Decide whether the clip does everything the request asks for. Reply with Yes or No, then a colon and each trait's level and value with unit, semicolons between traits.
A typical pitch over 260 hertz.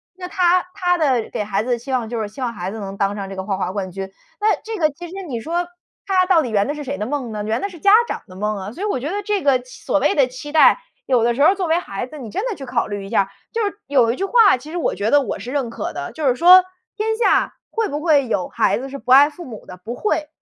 Yes: very high, 270 Hz